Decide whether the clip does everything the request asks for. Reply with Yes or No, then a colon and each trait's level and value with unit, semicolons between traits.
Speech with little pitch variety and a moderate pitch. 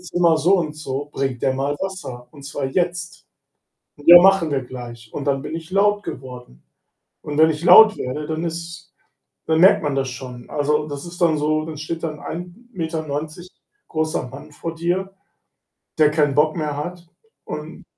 No: average, 3.4 semitones; medium, 155 Hz